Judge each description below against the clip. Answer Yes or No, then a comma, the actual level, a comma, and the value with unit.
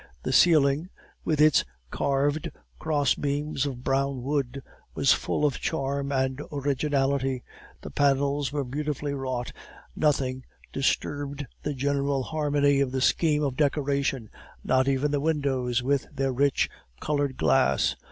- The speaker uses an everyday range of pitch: No, narrow, 1.6 semitones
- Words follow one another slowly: Yes, slow, 130 wpm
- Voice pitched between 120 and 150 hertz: Yes, medium, 140 Hz